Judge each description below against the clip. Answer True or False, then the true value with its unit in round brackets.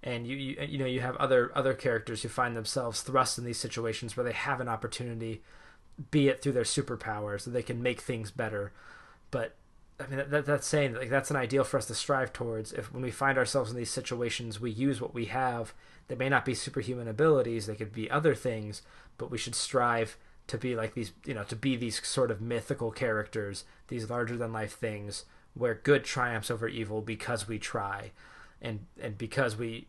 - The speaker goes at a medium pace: False (215 wpm)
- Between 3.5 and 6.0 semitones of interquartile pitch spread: False (2.9 semitones)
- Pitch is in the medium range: False (120 Hz)